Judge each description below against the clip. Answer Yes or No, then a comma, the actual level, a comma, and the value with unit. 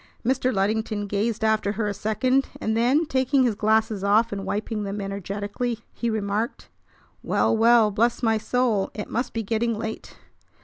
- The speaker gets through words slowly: No, average, 165 wpm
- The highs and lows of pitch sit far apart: No, narrow, 2.4 semitones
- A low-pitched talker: No, high, 220 Hz